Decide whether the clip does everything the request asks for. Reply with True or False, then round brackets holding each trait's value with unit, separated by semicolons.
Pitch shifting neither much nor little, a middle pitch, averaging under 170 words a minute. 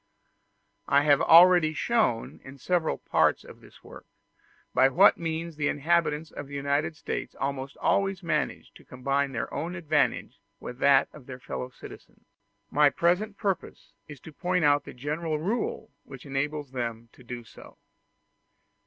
True (3.7 semitones; 150 Hz; 155 wpm)